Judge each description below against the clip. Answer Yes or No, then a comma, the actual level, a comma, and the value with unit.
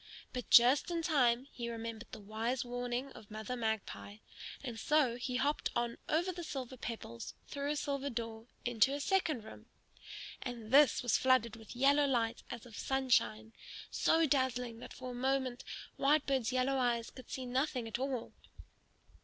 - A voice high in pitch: Yes, very high, 250 Hz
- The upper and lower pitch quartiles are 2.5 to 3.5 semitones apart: Yes, average, 2.8 semitones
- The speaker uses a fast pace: No, average, 165 wpm